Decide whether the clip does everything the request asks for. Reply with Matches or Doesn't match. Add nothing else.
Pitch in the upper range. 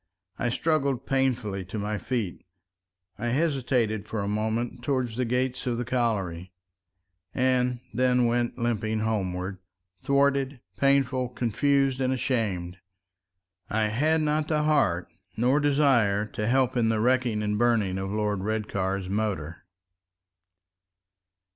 Doesn't match